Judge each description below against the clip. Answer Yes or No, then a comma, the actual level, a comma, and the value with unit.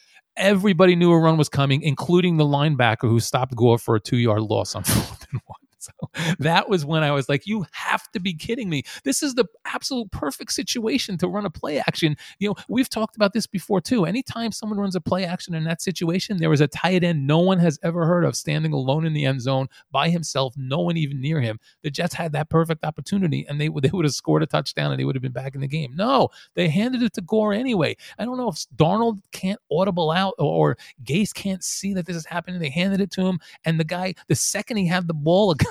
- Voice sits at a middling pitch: Yes, medium, 170 Hz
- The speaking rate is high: Yes, fast, 250 wpm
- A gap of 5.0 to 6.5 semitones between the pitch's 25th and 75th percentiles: Yes, wide, 5.5 semitones